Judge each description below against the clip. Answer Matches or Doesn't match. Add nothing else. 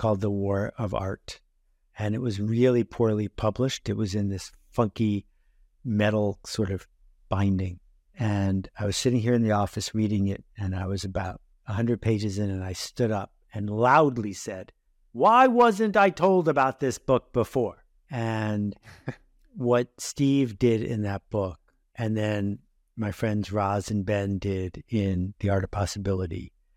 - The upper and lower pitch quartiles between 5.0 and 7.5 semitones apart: Doesn't match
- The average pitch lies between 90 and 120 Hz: Matches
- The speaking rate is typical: Matches